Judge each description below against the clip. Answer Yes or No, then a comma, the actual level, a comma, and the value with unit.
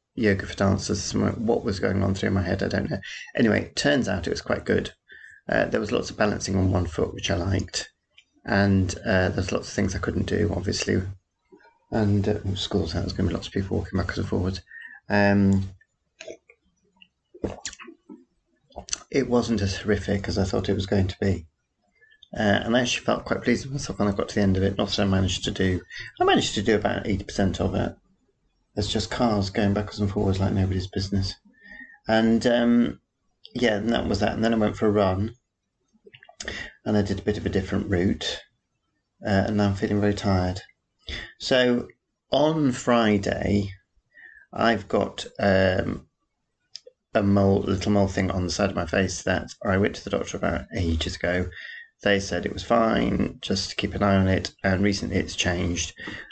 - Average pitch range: No, narrow, 1.8 semitones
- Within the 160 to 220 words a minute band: Yes, average, 195 wpm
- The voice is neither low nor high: No, low, 100 Hz